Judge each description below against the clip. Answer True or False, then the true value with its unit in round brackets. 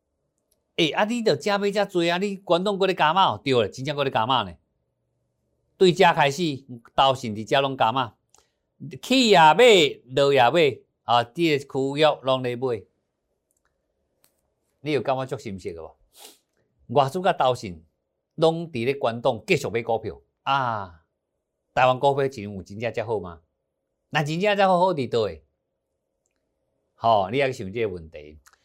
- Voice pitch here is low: True (130 Hz)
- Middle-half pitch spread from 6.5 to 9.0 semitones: True (8.0 semitones)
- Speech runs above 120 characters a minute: True (220 characters per minute)